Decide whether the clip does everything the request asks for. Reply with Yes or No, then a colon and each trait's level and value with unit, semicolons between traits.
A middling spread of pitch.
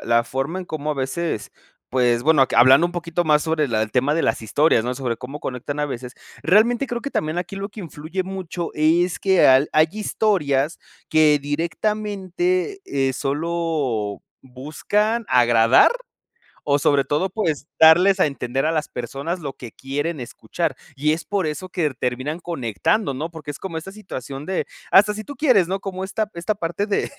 No: wide, 5.7 semitones